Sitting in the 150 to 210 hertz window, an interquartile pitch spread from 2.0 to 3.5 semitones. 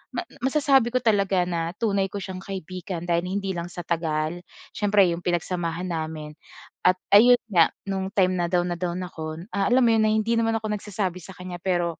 Yes: medium, 185 Hz; average, 3.0 semitones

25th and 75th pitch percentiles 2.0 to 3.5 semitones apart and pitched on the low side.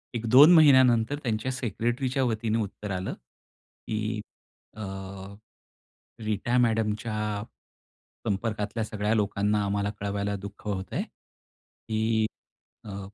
Yes: narrow, 2.4 semitones; low, 110 Hz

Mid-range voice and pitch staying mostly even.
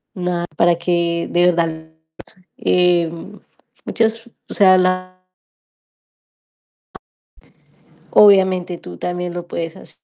Yes: medium, 175 Hz; narrow, 1.4 semitones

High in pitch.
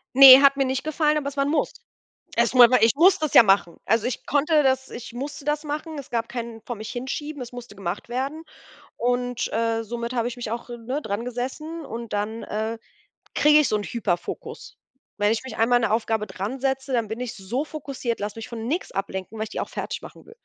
Yes: high, 245 Hz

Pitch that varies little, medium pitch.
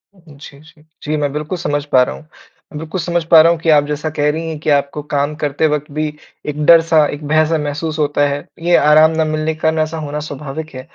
Yes: narrow, 1.5 semitones; medium, 155 Hz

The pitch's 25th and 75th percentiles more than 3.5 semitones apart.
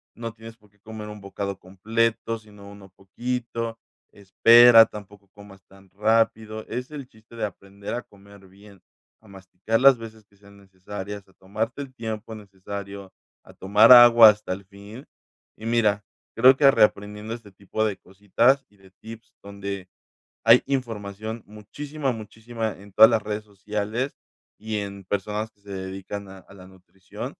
No: narrow, 2.4 semitones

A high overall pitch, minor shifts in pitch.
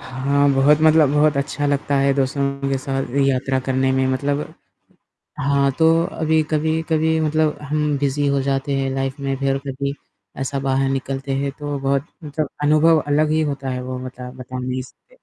No: medium, 140 Hz; narrow, 2.0 semitones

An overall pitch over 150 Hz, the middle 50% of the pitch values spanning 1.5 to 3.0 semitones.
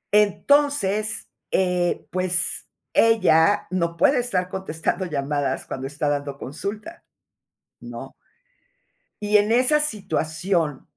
No: medium, 185 Hz; average, 5.1 semitones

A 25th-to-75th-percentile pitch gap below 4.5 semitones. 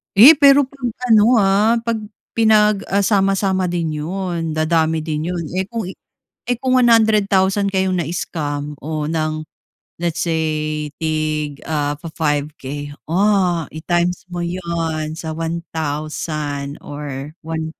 Yes: average, 4.1 semitones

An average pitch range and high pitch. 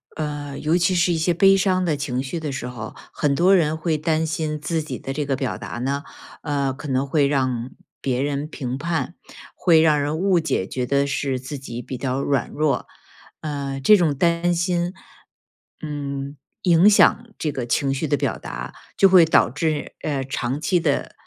No: average, 3.4 semitones; medium, 145 Hz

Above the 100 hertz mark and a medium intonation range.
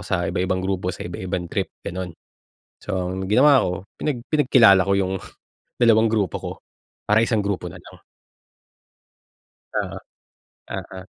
No: very low, 95 Hz; average, 3.6 semitones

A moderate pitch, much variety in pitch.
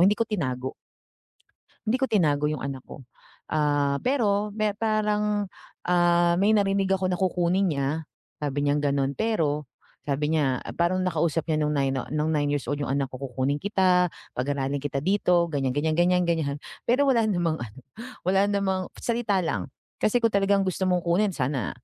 Yes: medium, 170 Hz; wide, 5.7 semitones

